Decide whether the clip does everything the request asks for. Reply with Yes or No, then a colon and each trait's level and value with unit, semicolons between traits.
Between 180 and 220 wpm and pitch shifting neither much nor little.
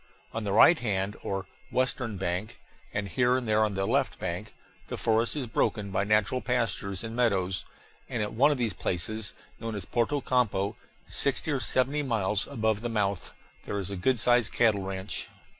Yes: average, 185 wpm; average, 3.8 semitones